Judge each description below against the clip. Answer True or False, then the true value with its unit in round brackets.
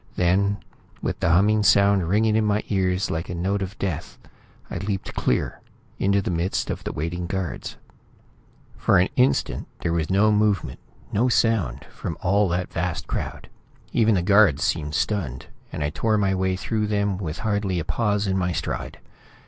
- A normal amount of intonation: True (3.0 semitones)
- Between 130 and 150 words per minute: False (175 wpm)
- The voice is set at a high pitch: False (95 Hz)